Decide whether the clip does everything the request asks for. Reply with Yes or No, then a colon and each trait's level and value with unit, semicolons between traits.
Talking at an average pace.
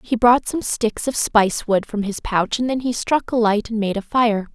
No: fast, 265 wpm